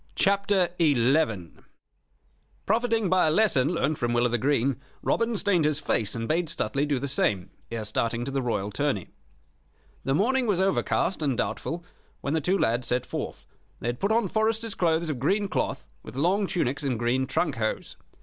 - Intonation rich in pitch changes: Yes, wide, 7.9 semitones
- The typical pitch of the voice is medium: Yes, medium, 150 Hz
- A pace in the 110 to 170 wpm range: No, average, 185 wpm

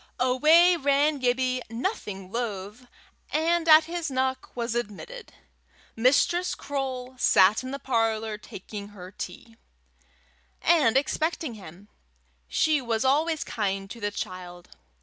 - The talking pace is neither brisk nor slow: No, slow, 120 wpm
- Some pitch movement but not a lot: No, wide, 6.1 semitones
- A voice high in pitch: Yes, very high, 250 Hz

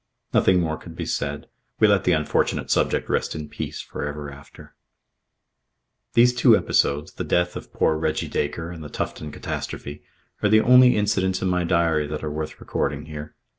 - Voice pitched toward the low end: Yes, very low, 80 Hz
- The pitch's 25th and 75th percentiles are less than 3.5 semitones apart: No, average, 3.9 semitones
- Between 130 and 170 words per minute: No, average, 180 wpm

